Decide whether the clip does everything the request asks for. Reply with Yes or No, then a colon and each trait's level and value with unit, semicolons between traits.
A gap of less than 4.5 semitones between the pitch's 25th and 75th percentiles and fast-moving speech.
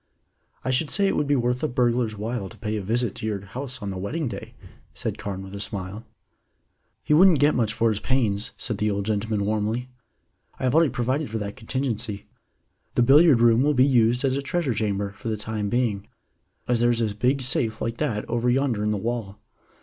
Yes: average, 3.5 semitones; fast, 220 wpm